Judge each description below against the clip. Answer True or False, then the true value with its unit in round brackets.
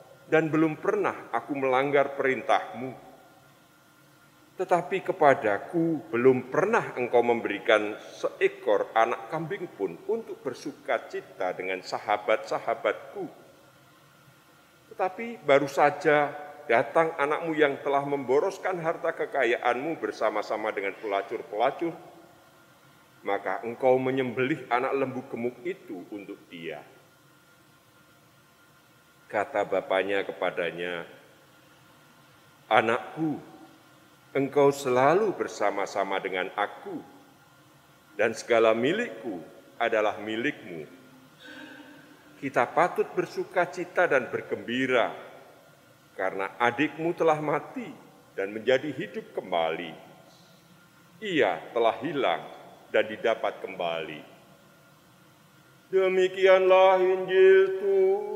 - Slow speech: True (80 wpm)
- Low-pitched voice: False (160 Hz)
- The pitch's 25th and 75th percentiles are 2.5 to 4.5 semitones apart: False (5.0 semitones)